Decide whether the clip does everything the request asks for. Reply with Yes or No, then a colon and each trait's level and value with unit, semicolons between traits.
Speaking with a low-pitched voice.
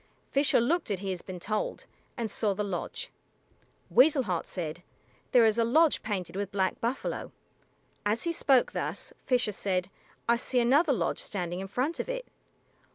No: high, 220 Hz